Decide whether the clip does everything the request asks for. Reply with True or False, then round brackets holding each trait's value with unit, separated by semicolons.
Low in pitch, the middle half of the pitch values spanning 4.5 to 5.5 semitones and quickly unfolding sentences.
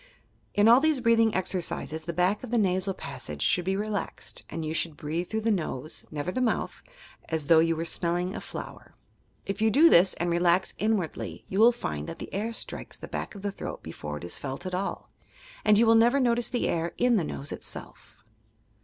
False (185 Hz; 5.2 semitones; 215 wpm)